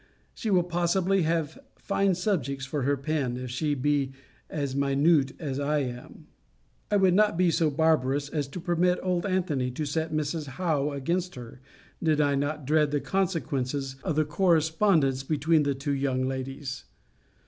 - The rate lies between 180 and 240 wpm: No, average, 165 wpm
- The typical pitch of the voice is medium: Yes, medium, 150 Hz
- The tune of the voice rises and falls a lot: No, average, 3.8 semitones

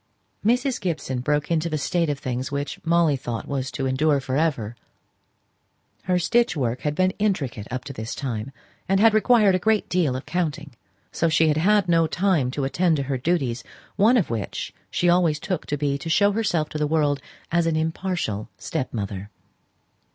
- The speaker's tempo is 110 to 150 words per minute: No, average, 185 wpm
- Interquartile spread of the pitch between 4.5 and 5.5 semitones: Yes, average, 5.1 semitones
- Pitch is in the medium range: Yes, medium, 155 Hz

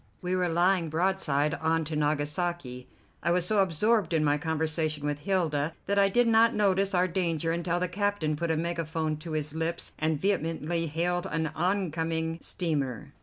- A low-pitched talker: No, medium, 165 Hz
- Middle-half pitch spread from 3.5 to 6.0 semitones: No, average, 2.8 semitones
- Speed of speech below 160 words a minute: No, average, 170 wpm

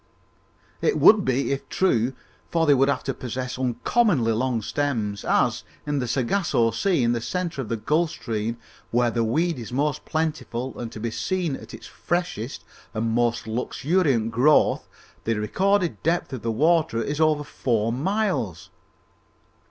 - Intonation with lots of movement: Yes, wide, 5.9 semitones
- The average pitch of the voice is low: Yes, low, 130 Hz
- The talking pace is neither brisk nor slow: Yes, average, 160 wpm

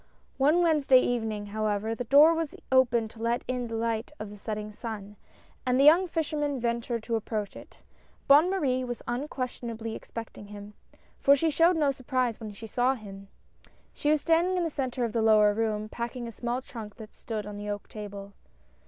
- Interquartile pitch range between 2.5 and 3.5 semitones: No, average, 4.2 semitones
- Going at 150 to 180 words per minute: No, fast, 205 wpm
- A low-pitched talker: No, high, 235 Hz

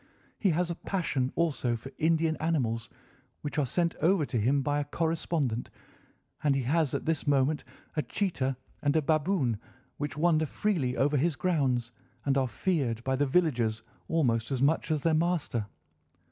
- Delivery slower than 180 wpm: Yes, average, 170 wpm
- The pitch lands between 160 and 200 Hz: No, medium, 145 Hz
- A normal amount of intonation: Yes, average, 4.0 semitones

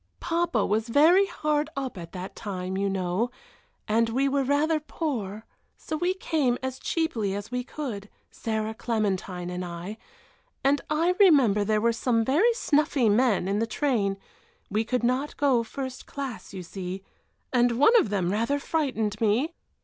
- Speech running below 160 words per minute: No, average, 165 wpm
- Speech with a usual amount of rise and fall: No, wide, 5.9 semitones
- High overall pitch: Yes, high, 235 Hz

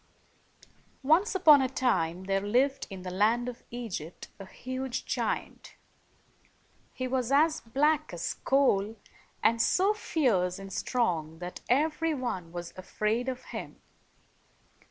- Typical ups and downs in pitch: No, wide, 6.3 semitones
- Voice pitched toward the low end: No, high, 240 Hz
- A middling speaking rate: No, slow, 130 wpm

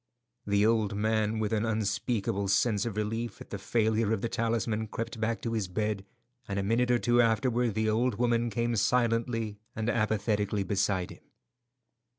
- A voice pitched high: No, low, 110 Hz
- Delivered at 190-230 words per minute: No, average, 170 wpm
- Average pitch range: No, narrow, 2.1 semitones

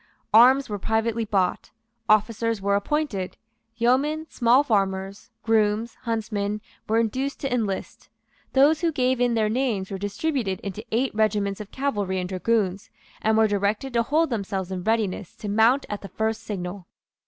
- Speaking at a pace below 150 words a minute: No, average, 155 wpm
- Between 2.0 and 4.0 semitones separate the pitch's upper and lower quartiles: Yes, average, 3.4 semitones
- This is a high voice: Yes, high, 220 Hz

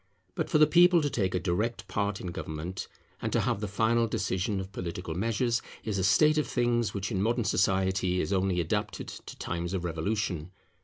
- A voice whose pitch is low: Yes, low, 100 Hz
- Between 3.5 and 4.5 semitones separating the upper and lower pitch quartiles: Yes, average, 4.1 semitones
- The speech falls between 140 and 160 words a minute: No, average, 200 wpm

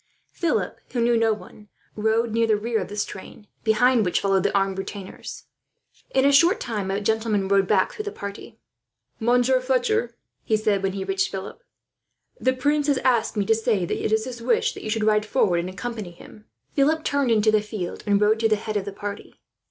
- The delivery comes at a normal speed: No, fast, 215 wpm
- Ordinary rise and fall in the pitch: Yes, average, 3.1 semitones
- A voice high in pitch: Yes, high, 220 Hz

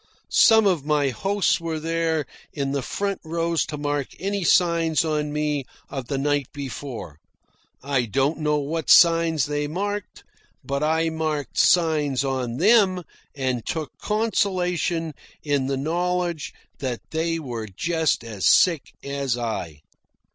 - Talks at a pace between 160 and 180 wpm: No, average, 140 wpm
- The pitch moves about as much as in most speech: Yes, average, 3.4 semitones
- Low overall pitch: No, medium, 150 Hz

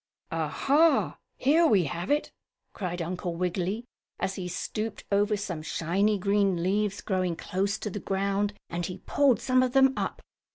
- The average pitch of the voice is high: Yes, high, 200 Hz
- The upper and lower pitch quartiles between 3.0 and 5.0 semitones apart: Yes, average, 3.3 semitones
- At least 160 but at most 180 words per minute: Yes, average, 165 wpm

